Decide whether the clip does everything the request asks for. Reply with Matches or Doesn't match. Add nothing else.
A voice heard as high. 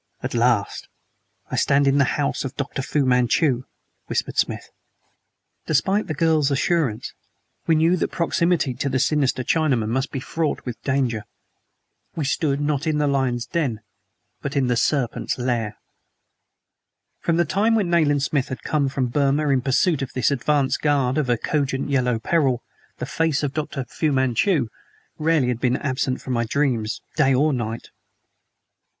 Doesn't match